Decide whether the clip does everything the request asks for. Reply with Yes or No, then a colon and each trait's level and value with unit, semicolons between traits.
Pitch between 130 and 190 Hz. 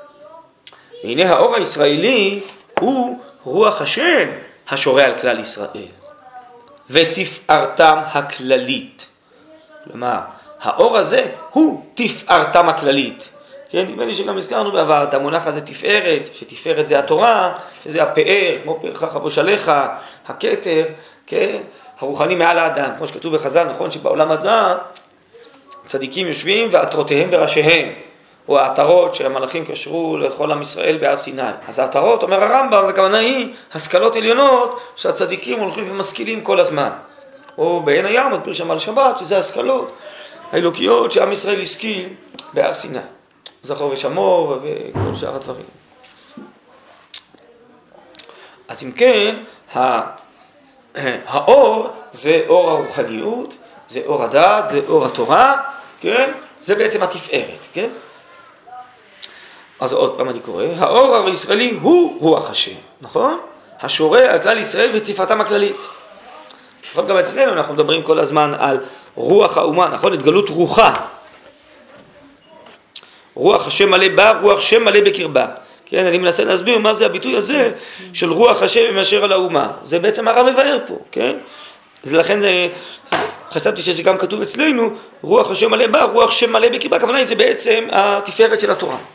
No: very high, 280 Hz